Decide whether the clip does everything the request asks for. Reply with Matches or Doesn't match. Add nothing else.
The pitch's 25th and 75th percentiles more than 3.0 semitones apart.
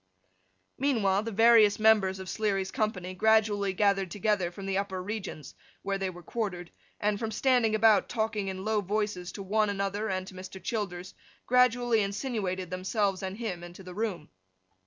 Doesn't match